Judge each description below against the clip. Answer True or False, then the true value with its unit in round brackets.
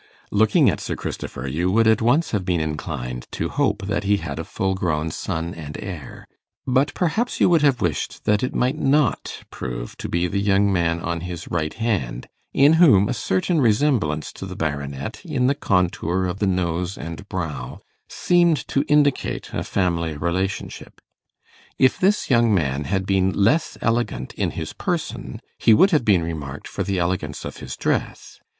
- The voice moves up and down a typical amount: False (6.2 semitones)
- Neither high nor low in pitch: False (95 Hz)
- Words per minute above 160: True (180 wpm)